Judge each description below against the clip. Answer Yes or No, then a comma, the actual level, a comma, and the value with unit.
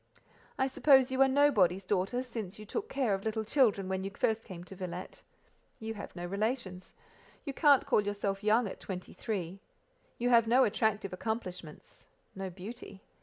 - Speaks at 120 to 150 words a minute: No, average, 170 wpm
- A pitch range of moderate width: Yes, average, 4.4 semitones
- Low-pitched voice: No, high, 210 Hz